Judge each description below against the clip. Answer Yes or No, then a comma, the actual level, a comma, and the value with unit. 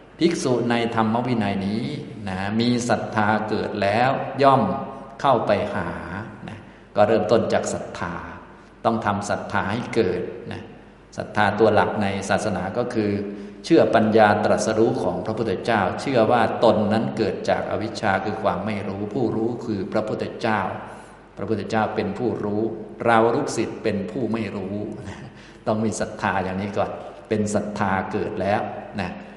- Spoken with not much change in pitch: Yes, narrow, 1.6 semitones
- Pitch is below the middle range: Yes, low, 105 Hz